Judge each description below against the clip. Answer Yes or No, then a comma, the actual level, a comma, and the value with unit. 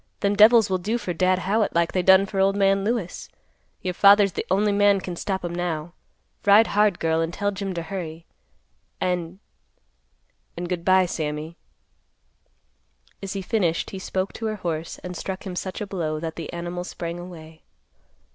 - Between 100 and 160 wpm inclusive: No, average, 175 wpm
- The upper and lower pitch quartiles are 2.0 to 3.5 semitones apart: Yes, average, 2.7 semitones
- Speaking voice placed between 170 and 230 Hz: Yes, medium, 185 Hz